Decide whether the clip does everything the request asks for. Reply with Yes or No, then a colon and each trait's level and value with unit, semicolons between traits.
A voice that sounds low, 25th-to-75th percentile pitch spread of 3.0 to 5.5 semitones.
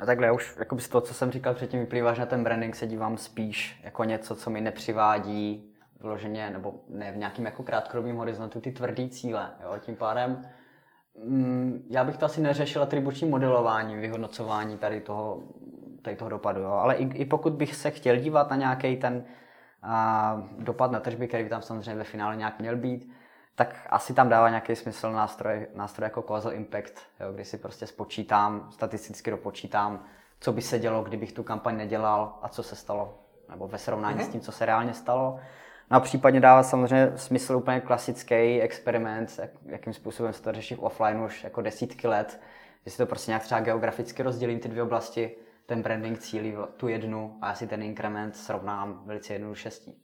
No: low, 115 Hz; narrow, 2.5 semitones